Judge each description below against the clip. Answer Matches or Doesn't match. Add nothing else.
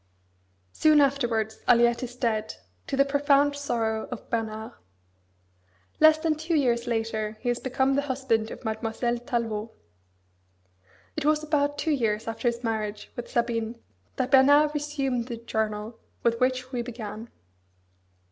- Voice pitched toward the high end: Matches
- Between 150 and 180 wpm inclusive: Doesn't match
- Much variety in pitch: Doesn't match